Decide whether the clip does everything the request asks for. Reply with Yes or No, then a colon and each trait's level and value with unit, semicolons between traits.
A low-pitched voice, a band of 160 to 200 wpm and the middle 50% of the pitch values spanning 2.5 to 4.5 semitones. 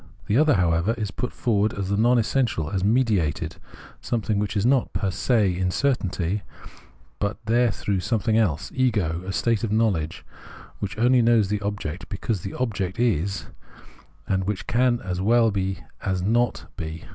Yes: low, 105 Hz; average, 175 wpm; average, 3.7 semitones